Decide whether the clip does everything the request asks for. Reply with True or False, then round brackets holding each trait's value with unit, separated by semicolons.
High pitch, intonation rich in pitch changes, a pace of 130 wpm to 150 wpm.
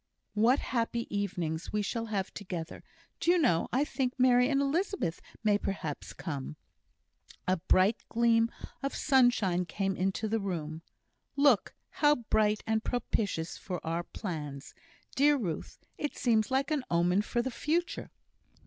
True (215 Hz; 6.0 semitones; 145 wpm)